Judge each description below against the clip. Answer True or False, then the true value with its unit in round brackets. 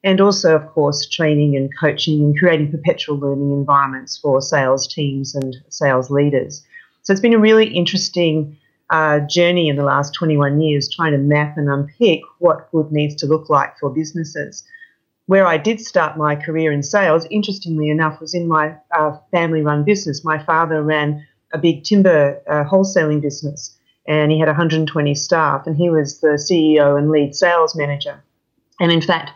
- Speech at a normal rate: True (180 wpm)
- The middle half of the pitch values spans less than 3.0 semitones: True (2.6 semitones)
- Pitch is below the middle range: False (155 Hz)